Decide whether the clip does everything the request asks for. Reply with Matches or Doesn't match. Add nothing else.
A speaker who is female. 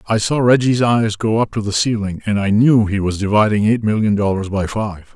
Doesn't match